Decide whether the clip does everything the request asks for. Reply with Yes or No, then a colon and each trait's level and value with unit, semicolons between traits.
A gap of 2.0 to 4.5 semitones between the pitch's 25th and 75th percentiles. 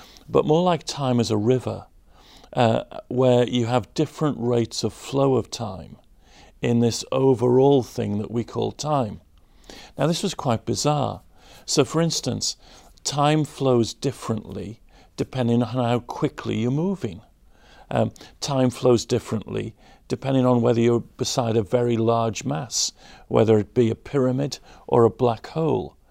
Yes: average, 3.0 semitones